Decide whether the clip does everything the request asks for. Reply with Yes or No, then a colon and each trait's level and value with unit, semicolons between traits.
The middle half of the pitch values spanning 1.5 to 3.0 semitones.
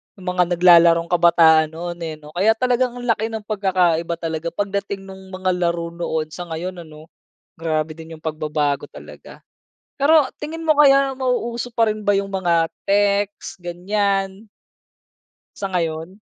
No: average, 4.0 semitones